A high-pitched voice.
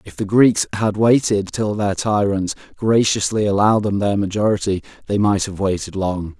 No: low, 100 Hz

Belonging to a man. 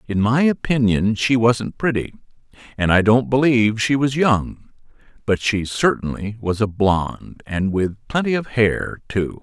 Yes: male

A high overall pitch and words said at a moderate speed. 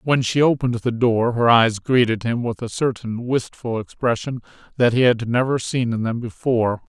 No: low, 120 Hz; average, 190 wpm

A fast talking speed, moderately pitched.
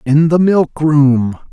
No: average, 160 wpm; medium, 150 Hz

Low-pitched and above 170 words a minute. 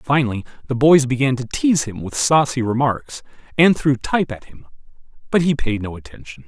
Yes: low, 130 Hz; average, 185 wpm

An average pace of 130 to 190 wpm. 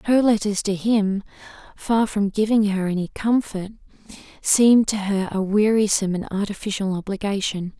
Yes: average, 140 wpm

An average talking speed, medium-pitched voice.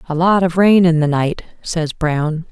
No: fast, 215 wpm; medium, 165 Hz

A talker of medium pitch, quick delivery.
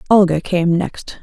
No: medium, 180 Hz; average, 145 wpm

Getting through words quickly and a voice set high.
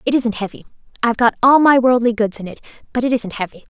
Yes: fast, 240 wpm; high, 235 Hz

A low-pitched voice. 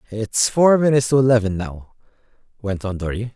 Yes: low, 115 Hz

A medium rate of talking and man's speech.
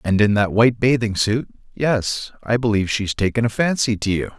Yes: average, 190 wpm; male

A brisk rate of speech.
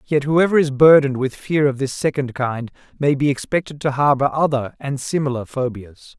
No: average, 185 wpm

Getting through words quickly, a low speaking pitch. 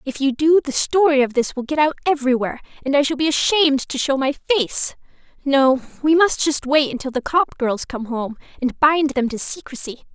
No: fast, 215 wpm; very high, 280 Hz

